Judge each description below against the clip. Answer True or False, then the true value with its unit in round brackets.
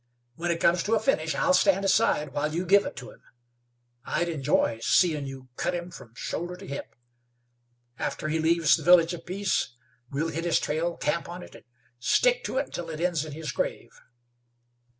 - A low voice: False (170 Hz)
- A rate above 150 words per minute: True (195 wpm)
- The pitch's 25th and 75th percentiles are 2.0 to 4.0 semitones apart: True (2.9 semitones)